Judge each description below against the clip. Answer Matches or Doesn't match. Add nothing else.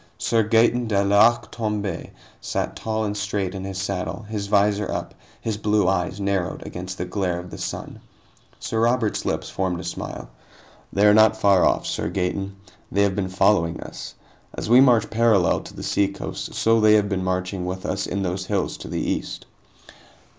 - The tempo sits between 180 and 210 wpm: Matches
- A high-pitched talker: Doesn't match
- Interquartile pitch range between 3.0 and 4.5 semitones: Doesn't match